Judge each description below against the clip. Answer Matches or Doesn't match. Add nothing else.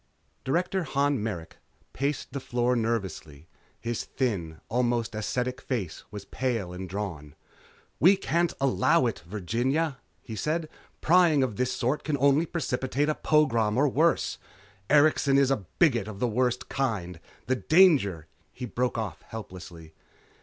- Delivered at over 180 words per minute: Doesn't match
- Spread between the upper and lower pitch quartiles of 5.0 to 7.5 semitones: Matches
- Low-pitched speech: Matches